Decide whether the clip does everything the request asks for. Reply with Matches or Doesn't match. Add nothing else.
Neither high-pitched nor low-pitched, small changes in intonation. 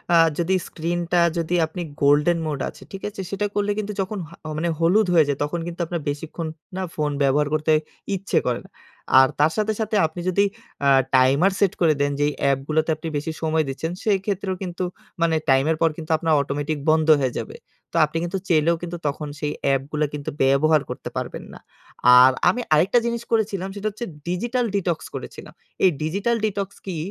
Doesn't match